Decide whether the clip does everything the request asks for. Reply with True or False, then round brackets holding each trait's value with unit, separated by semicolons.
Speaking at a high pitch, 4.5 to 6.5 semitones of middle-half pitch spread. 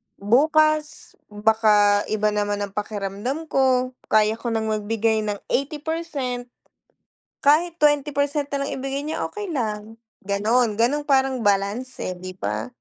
True (235 Hz; 5.3 semitones)